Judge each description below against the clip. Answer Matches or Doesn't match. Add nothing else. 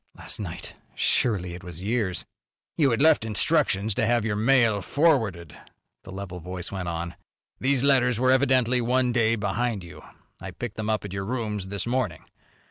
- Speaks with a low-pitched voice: Matches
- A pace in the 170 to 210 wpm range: Matches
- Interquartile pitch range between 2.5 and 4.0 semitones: Doesn't match